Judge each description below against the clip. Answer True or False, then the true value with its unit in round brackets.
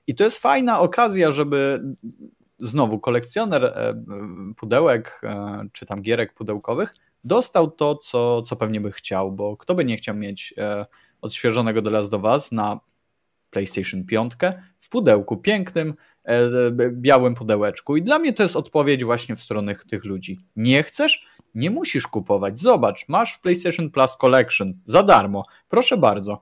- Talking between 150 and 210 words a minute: True (155 wpm)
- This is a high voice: False (120 Hz)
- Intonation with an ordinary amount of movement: False (6.9 semitones)